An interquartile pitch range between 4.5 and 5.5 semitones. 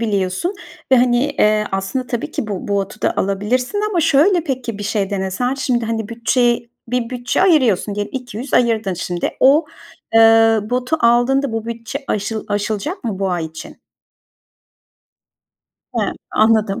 No: average, 3.8 semitones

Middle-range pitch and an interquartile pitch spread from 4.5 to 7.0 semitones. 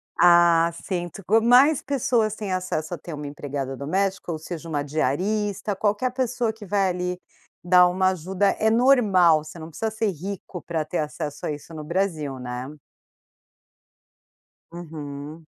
Yes: medium, 180 Hz; average, 4.8 semitones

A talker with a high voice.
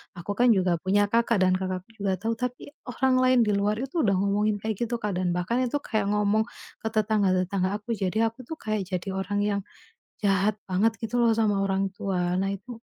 Yes: high, 205 Hz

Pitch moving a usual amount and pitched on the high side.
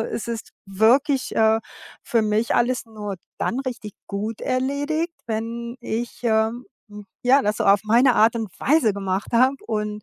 Yes: average, 3.0 semitones; high, 225 Hz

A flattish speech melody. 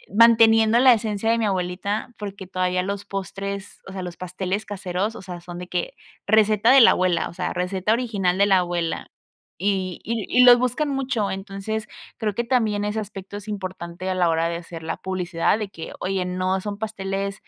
No: average, 3.0 semitones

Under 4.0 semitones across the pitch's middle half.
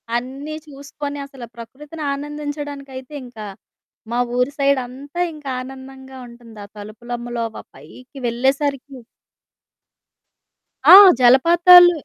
Yes: average, 3.0 semitones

